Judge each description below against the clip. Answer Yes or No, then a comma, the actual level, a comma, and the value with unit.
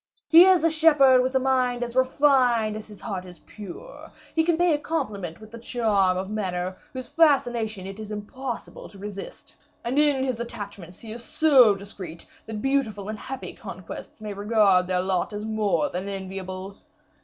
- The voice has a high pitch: Yes, high, 220 Hz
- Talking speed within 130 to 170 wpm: No, average, 180 wpm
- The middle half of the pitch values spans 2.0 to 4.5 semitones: No, average, 4.9 semitones